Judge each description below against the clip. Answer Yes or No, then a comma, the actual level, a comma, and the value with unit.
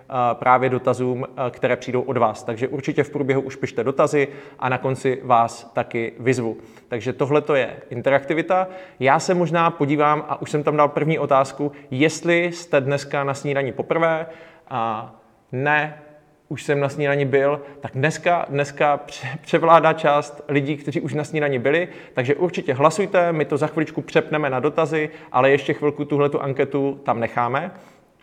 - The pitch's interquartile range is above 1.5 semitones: Yes, average, 2.7 semitones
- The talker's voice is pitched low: No, medium, 145 Hz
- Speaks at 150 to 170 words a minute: Yes, average, 160 wpm